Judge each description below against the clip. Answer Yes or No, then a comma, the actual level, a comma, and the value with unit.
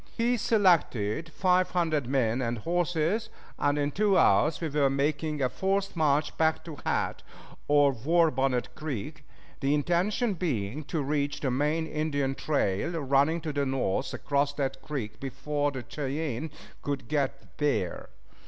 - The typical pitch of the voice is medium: Yes, medium, 145 Hz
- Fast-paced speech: No, average, 150 wpm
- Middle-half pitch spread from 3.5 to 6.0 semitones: No, average, 3.1 semitones